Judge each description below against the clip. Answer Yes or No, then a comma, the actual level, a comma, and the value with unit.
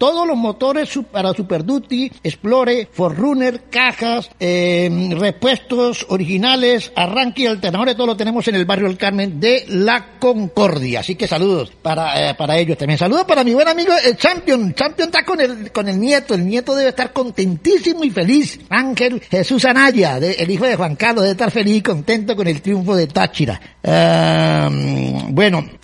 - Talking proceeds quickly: No, average, 175 wpm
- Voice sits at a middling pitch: No, high, 225 Hz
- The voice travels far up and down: Yes, wide, 5.9 semitones